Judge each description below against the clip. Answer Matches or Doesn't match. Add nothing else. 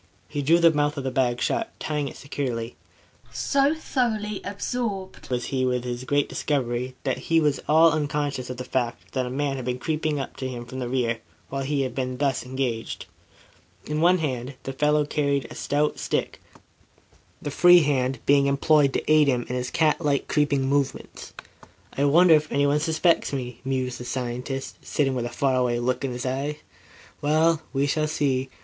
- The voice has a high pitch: Doesn't match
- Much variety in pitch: Doesn't match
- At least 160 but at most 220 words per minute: Matches